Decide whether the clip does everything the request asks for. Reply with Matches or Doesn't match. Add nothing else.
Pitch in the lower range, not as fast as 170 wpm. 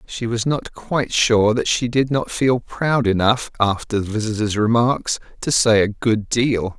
Doesn't match